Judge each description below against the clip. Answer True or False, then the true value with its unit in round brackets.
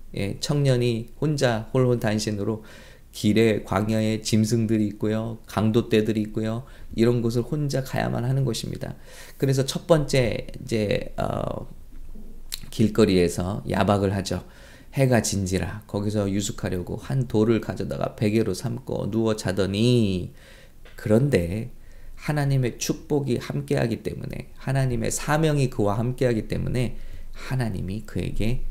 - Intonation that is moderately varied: True (3.5 semitones)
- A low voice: True (115 Hz)